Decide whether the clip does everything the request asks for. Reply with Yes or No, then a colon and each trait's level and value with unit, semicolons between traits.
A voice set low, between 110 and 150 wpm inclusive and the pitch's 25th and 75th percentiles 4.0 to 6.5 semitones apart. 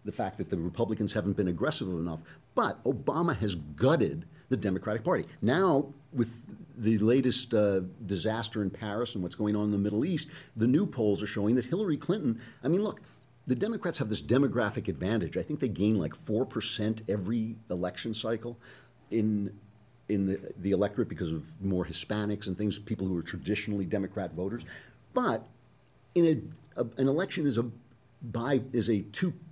No: low, 110 Hz; average, 180 wpm; average, 4.3 semitones